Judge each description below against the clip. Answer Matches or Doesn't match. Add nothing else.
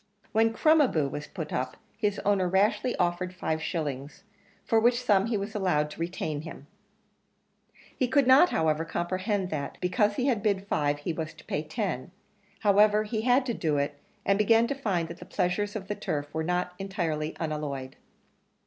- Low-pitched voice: Doesn't match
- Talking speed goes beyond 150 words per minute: Matches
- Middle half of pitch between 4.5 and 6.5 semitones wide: Matches